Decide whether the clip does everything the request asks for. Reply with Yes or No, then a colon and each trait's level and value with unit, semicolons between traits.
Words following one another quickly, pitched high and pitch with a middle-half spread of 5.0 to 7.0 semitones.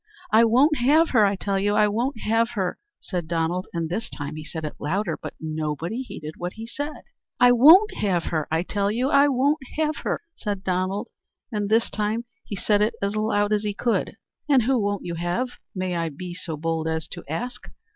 Yes: fast, 210 wpm; high, 205 Hz; wide, 5.4 semitones